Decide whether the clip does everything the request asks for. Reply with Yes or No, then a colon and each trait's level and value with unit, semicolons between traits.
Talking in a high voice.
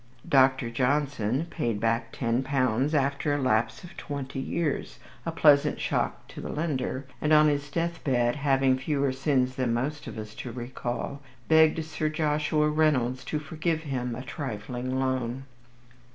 No: low, 135 Hz